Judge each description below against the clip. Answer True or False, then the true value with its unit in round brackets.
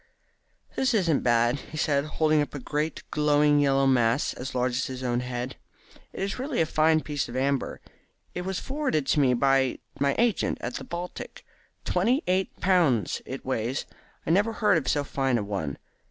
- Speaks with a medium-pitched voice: True (145 Hz)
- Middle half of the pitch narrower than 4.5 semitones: False (5.1 semitones)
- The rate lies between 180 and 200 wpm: True (190 wpm)